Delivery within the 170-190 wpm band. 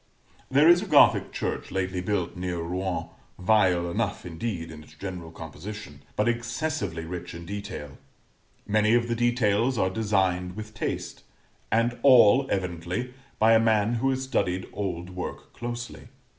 No: average, 150 wpm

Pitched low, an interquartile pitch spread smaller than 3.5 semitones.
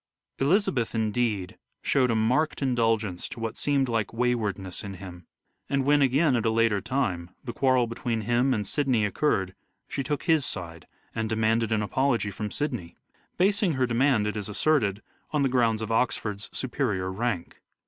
No: low, 115 Hz; average, 4.2 semitones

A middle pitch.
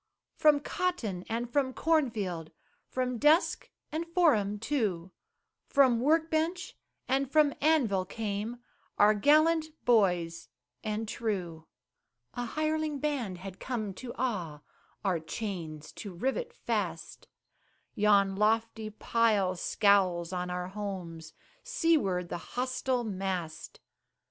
No: high, 220 Hz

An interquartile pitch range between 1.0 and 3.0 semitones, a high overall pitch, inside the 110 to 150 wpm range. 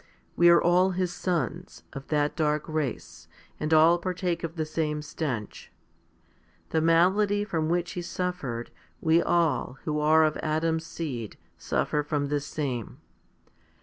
No: narrow, 2.5 semitones; medium, 160 Hz; average, 145 wpm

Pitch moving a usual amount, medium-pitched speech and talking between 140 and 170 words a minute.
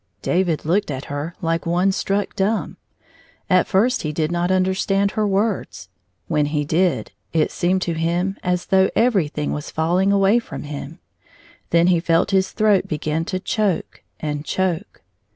Yes: average, 3.3 semitones; medium, 180 Hz; average, 165 wpm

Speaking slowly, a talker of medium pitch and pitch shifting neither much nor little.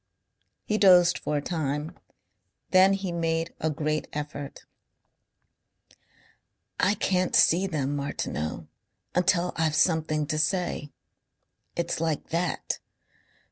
Yes: slow, 105 wpm; medium, 165 Hz; average, 3.1 semitones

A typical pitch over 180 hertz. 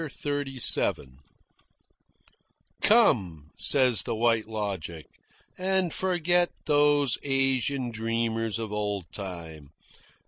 No: low, 115 Hz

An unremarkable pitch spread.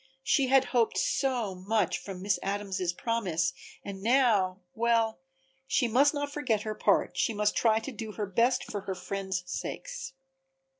Yes: average, 4.1 semitones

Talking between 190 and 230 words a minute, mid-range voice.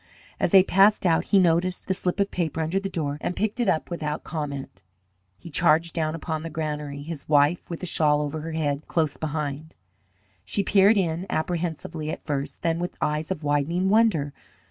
Yes: average, 195 wpm; medium, 160 Hz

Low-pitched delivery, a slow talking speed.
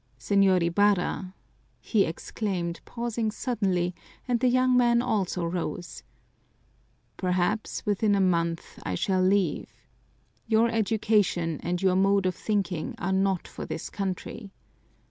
No: high, 195 Hz; slow, 125 wpm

